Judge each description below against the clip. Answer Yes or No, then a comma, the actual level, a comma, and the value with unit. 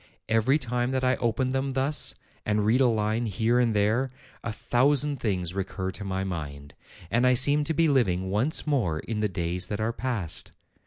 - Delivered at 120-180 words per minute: No, average, 195 wpm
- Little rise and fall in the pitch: No, average, 5.1 semitones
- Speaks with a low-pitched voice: Yes, low, 115 Hz